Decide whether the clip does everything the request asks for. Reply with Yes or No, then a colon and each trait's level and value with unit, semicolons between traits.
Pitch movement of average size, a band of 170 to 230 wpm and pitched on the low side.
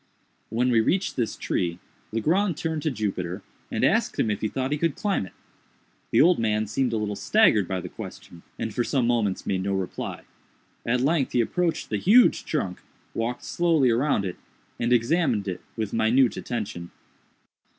No: wide, 6.2 semitones; average, 180 wpm; low, 115 Hz